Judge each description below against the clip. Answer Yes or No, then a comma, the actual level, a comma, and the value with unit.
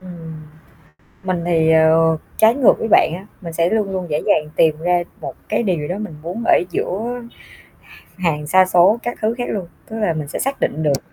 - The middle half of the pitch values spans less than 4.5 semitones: No, average, 4.8 semitones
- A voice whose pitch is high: No, medium, 175 Hz